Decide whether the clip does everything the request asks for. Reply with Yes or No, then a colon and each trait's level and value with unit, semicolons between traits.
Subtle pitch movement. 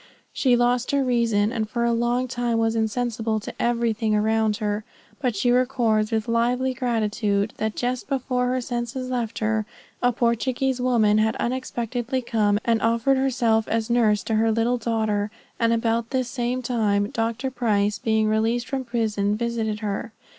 Yes: narrow, 2.1 semitones